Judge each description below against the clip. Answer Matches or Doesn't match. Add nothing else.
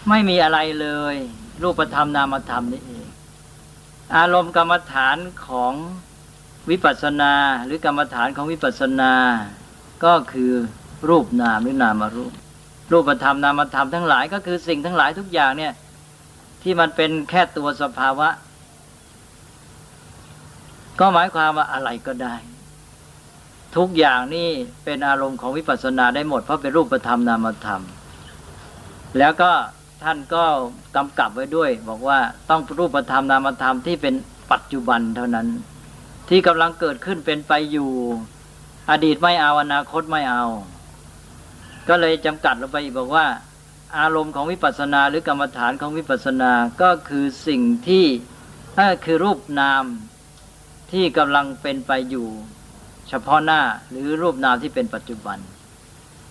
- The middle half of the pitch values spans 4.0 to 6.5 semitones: Matches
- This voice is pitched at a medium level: Matches